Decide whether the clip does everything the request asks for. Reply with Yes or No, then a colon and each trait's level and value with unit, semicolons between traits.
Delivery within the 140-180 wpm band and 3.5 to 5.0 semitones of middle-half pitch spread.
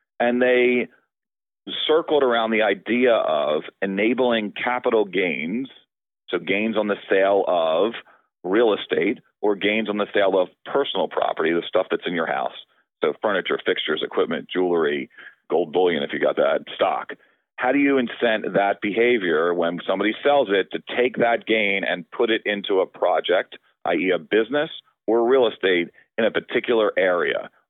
Yes: average, 160 wpm; average, 3.8 semitones